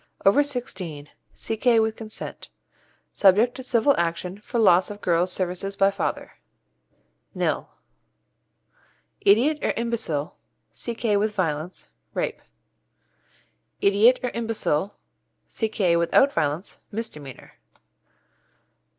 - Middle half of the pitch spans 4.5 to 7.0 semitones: Yes, average, 5.0 semitones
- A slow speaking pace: Yes, slow, 100 wpm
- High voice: Yes, high, 200 Hz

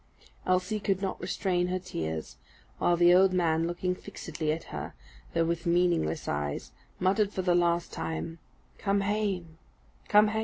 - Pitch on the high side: No, medium, 175 Hz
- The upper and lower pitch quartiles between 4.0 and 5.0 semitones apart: No, narrow, 2.5 semitones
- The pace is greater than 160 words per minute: No, average, 155 wpm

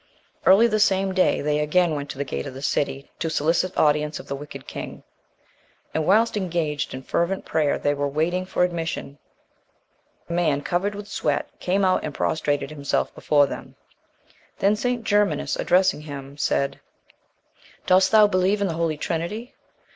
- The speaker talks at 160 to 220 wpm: Yes, average, 170 wpm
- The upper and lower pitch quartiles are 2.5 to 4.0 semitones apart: No, average, 4.5 semitones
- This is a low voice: No, medium, 170 Hz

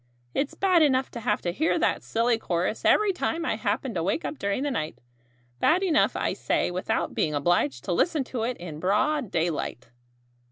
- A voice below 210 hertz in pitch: No, high, 225 Hz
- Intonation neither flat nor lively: No, wide, 9.0 semitones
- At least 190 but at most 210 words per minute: Yes, average, 195 wpm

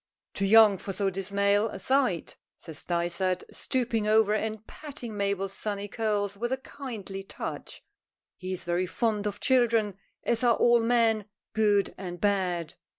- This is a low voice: No, high, 205 Hz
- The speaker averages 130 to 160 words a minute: Yes, average, 150 wpm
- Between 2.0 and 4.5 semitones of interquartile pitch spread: Yes, average, 2.8 semitones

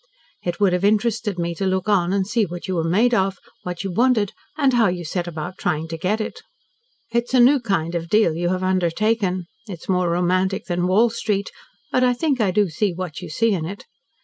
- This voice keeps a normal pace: No, fast, 225 wpm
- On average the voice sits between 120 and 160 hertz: No, high, 190 Hz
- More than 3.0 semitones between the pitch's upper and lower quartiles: Yes, average, 3.6 semitones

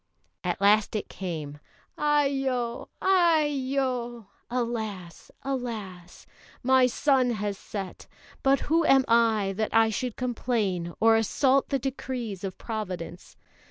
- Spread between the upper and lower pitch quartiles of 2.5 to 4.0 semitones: No, average, 4.6 semitones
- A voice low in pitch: No, high, 235 Hz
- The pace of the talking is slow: Yes, slow, 115 wpm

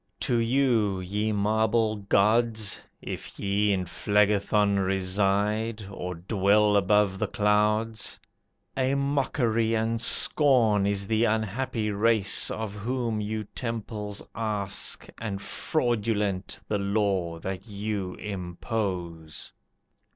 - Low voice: Yes, low, 105 Hz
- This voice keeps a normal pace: No, slow, 105 wpm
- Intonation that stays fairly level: Yes, narrow, 2.2 semitones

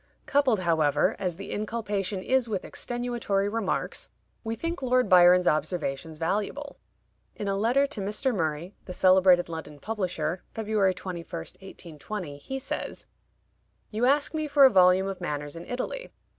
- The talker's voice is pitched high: Yes, high, 195 Hz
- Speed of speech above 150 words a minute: No, average, 145 wpm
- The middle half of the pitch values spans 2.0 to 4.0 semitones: No, average, 5.3 semitones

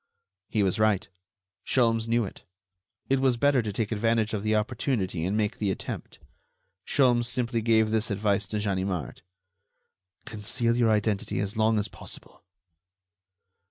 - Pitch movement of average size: No, narrow, 2.2 semitones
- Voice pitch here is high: No, low, 110 Hz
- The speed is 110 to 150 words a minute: Yes, average, 145 wpm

